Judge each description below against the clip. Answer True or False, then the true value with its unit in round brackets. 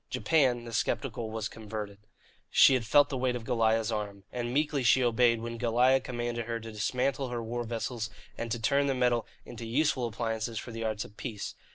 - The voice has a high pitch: False (120 Hz)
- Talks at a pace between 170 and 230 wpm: True (200 wpm)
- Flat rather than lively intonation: True (2.0 semitones)